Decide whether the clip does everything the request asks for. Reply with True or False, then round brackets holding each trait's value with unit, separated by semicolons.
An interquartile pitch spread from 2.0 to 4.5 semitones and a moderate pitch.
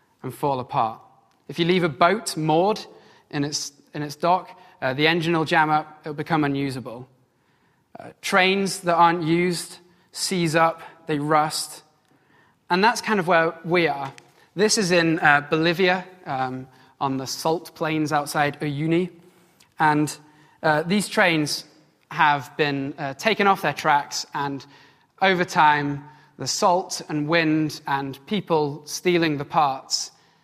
True (3.3 semitones; 155 Hz)